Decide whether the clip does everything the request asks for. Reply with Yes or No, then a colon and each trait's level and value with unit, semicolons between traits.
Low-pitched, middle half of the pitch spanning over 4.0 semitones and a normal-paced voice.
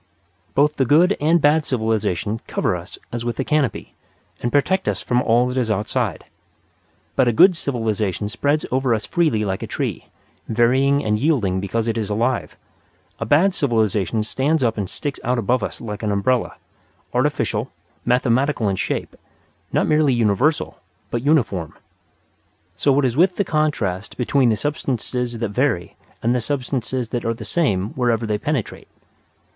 Yes: low, 120 Hz; average, 4.6 semitones; average, 165 wpm